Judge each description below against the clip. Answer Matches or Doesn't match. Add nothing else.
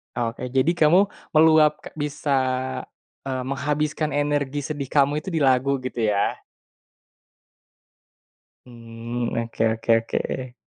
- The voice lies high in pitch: Doesn't match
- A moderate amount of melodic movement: Matches